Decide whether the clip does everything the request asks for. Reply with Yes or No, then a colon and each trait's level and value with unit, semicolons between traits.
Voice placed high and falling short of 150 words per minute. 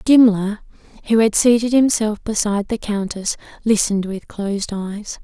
Yes: high, 210 Hz; average, 140 wpm